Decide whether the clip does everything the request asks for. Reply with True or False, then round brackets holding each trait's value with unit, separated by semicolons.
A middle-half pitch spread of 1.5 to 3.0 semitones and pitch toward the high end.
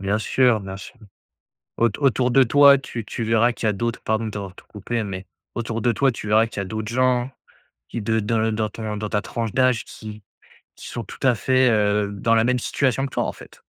False (2.7 semitones; 115 Hz)